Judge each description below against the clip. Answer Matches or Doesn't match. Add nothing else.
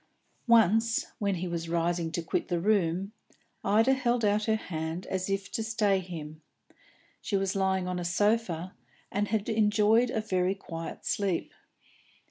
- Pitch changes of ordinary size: Matches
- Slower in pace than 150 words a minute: Doesn't match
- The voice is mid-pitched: Doesn't match